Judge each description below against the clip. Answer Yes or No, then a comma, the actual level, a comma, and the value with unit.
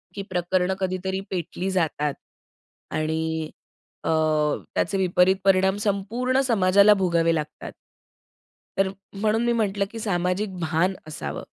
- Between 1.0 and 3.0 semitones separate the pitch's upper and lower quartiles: Yes, narrow, 2.6 semitones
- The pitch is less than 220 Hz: Yes, high, 190 Hz